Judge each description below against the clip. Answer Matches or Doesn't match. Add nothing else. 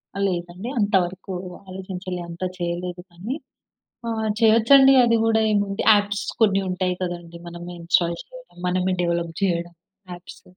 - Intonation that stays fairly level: Doesn't match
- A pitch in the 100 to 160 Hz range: Doesn't match